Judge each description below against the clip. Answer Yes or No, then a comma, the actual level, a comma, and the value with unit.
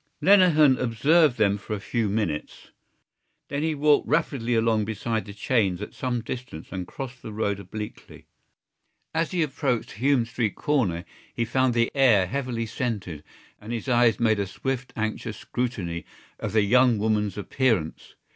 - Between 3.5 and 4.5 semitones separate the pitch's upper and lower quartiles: Yes, average, 3.9 semitones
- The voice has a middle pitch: No, low, 115 Hz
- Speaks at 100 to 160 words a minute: Yes, average, 155 wpm